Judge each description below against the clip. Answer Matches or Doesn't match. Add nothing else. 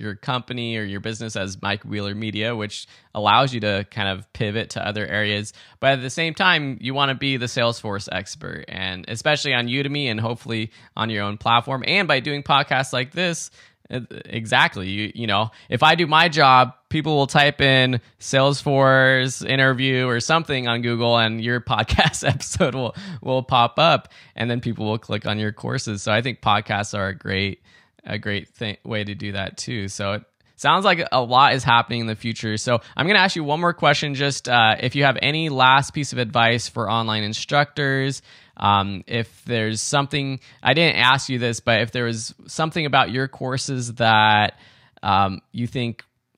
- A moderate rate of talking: Matches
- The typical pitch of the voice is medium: Doesn't match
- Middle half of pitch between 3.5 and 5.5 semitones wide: Matches